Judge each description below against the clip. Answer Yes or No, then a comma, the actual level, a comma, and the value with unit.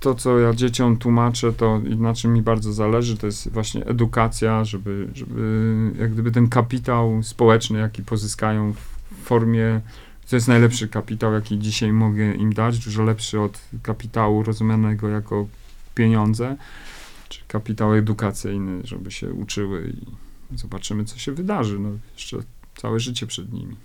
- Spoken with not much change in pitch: Yes, narrow, 1.6 semitones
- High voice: No, low, 110 Hz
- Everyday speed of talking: Yes, average, 150 wpm